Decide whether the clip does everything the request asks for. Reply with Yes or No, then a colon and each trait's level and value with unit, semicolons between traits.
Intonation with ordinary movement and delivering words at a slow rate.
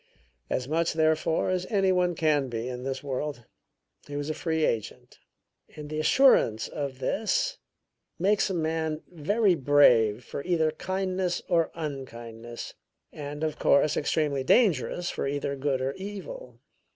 No: average, 4.6 semitones; average, 145 wpm